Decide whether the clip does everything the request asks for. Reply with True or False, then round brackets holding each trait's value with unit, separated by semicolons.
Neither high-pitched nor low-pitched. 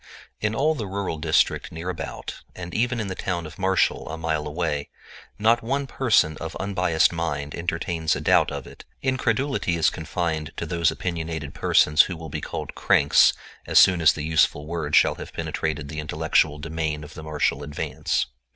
False (80 Hz)